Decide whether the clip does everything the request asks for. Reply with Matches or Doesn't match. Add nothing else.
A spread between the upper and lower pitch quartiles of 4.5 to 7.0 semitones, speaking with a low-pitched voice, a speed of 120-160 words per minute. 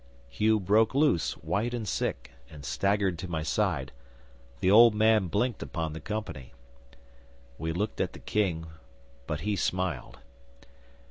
Matches